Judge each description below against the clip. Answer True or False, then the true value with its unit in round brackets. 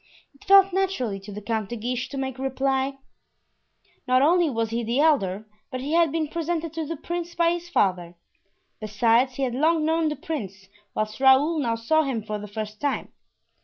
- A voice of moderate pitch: False (265 Hz)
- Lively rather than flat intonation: True (6.1 semitones)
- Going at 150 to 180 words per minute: False (195 wpm)